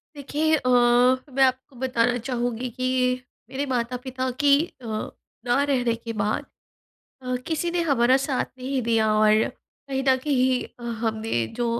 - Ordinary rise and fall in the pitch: No, narrow, 2.1 semitones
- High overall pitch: Yes, very high, 255 Hz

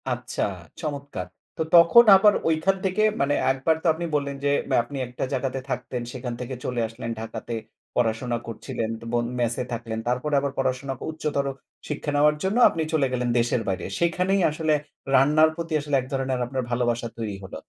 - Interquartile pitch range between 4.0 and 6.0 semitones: Yes, average, 4.4 semitones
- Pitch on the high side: No, low, 135 Hz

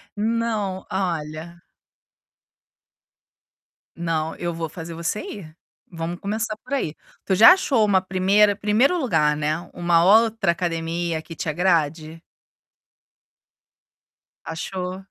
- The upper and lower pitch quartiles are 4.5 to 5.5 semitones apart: No, average, 4.1 semitones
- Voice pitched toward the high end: No, medium, 175 Hz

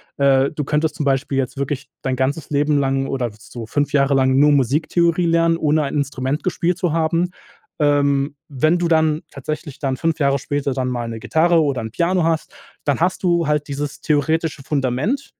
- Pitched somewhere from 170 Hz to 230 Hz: No, medium, 145 Hz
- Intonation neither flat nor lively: Yes, average, 3.0 semitones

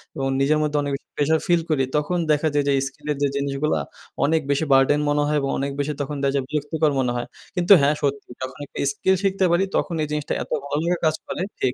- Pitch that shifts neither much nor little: No, narrow, 2.2 semitones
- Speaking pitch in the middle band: Yes, medium, 145 Hz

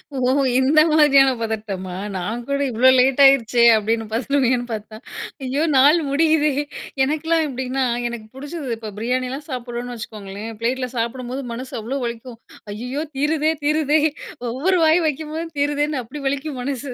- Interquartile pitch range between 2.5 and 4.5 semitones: Yes, average, 3.8 semitones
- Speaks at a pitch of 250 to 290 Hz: Yes, very high, 260 Hz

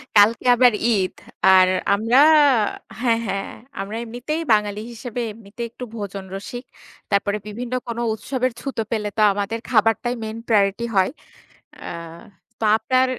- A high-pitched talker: Yes, high, 220 Hz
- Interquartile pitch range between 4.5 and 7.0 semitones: No, average, 3.0 semitones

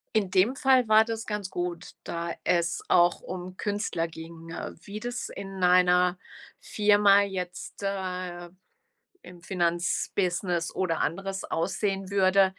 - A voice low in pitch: No, medium, 185 Hz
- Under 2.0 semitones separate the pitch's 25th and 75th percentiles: No, narrow, 2.4 semitones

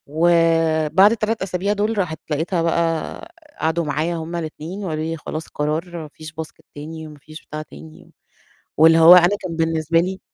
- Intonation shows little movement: Yes, narrow, 2.0 semitones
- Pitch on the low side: No, medium, 165 Hz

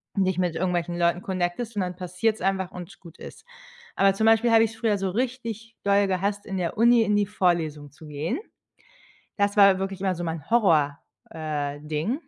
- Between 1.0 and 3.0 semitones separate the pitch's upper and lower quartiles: No, average, 3.5 semitones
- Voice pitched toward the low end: No, high, 190 Hz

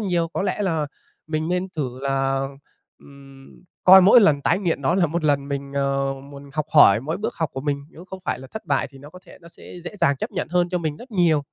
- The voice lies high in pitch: No, medium, 155 Hz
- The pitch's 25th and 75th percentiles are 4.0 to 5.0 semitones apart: Yes, average, 4.3 semitones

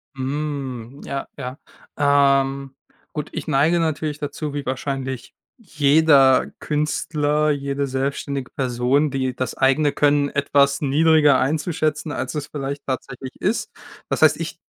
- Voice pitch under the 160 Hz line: Yes, medium, 140 Hz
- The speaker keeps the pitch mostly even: Yes, narrow, 1.9 semitones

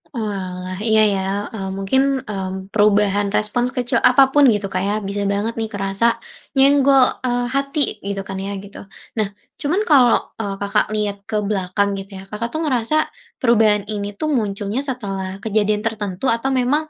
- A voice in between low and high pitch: No, high, 210 Hz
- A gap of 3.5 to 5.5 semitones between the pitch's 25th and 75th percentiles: Yes, average, 3.8 semitones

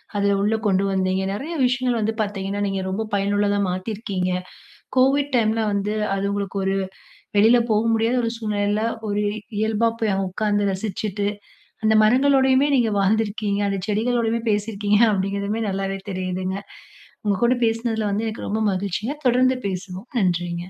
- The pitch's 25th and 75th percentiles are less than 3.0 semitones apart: Yes, narrow, 2.4 semitones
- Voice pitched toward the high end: Yes, high, 205 Hz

